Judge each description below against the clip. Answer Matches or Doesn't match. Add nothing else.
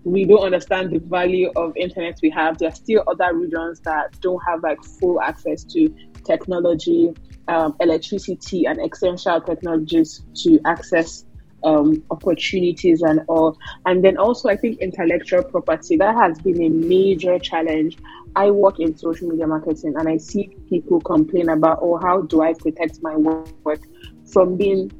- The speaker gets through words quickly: Doesn't match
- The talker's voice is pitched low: Doesn't match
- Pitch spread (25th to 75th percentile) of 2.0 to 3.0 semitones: Matches